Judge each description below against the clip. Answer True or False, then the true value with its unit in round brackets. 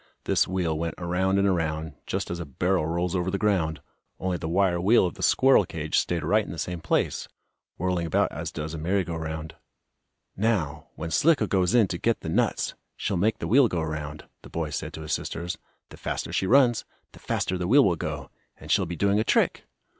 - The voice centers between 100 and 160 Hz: False (90 Hz)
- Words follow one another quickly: True (220 wpm)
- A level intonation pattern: False (3.6 semitones)